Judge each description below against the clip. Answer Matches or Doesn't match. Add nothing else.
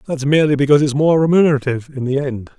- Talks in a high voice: Doesn't match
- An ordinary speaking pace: Doesn't match